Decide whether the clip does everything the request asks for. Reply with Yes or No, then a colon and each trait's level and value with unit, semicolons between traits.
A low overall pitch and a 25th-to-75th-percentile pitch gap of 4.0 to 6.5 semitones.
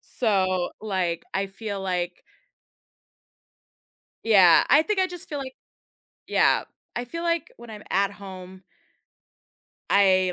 No: high, 200 Hz; average, 4.6 semitones